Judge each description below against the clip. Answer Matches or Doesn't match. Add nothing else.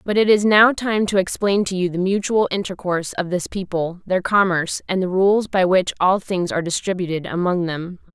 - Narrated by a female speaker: Matches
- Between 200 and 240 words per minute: Matches